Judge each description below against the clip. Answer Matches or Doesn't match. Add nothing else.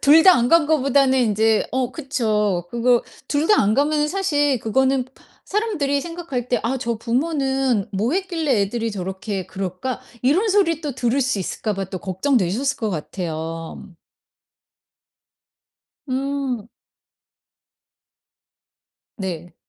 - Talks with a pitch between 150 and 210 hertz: Doesn't match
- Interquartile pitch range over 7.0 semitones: Doesn't match